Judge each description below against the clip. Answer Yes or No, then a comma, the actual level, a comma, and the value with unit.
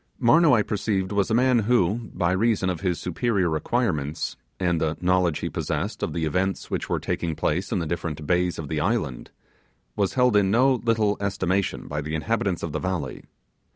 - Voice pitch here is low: Yes, very low, 95 Hz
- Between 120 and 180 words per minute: No, average, 190 wpm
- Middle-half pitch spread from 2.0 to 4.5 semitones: No, average, 5.1 semitones